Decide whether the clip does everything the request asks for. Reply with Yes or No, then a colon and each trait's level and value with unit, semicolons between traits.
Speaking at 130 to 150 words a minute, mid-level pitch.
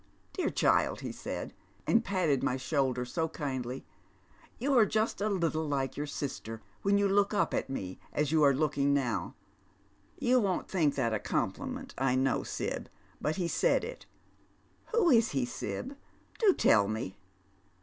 No: average, 170 wpm; medium, 150 Hz